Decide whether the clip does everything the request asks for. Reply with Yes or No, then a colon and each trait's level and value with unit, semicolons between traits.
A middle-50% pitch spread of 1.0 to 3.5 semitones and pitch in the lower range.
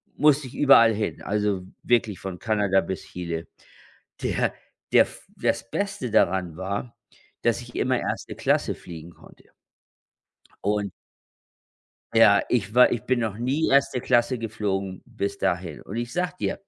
No: average, 4.1 semitones; low, 110 Hz